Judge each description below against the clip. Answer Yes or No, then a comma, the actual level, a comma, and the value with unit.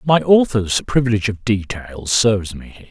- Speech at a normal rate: Yes, average, 165 wpm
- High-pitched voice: No, low, 110 Hz